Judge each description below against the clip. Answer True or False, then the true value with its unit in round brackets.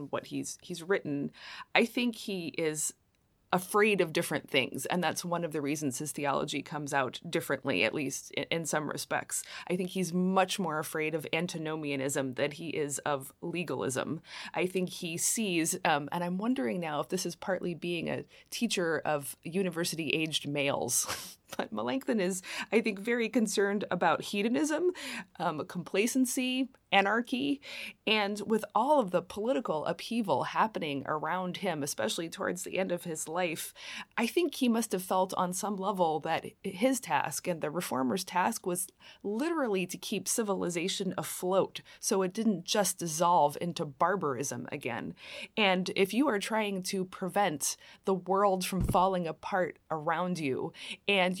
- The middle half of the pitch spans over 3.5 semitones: True (4.3 semitones)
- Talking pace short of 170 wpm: True (160 wpm)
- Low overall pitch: False (185 Hz)